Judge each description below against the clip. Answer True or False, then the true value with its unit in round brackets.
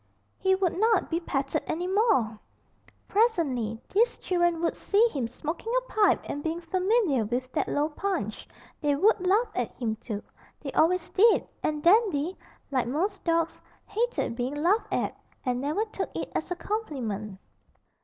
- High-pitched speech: True (335 Hz)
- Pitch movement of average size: False (7.0 semitones)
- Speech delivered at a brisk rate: False (160 wpm)